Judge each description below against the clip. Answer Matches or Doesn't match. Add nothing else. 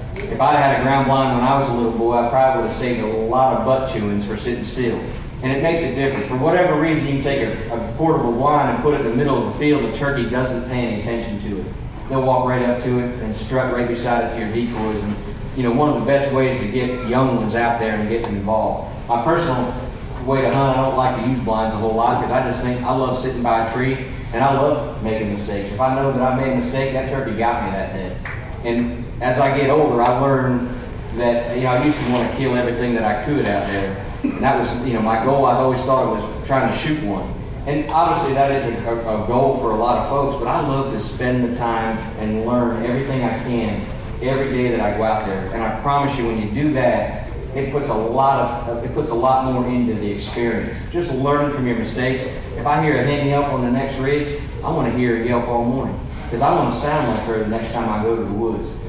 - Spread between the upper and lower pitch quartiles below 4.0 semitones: Matches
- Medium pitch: Doesn't match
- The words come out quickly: Matches